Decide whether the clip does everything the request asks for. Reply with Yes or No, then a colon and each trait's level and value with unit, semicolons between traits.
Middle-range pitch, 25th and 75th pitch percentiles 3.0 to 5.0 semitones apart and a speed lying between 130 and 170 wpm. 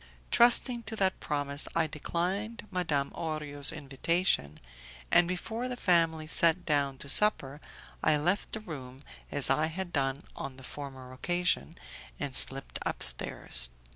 Yes: medium, 155 Hz; average, 4.6 semitones; average, 140 wpm